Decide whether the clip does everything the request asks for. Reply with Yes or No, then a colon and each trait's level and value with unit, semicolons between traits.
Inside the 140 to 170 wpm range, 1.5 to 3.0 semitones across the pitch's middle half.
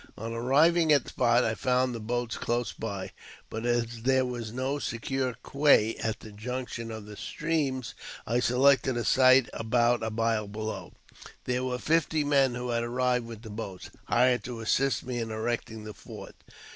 No: average, 180 wpm; narrow, 2.4 semitones